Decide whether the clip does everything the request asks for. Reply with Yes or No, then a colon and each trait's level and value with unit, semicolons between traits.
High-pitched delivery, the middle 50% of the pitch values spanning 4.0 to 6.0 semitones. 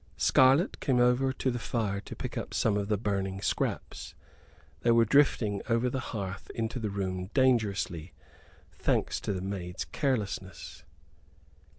No: low, 105 Hz; average, 4.3 semitones